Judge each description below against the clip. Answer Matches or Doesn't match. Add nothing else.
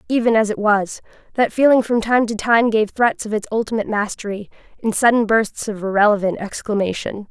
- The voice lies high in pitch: Matches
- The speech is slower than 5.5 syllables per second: Doesn't match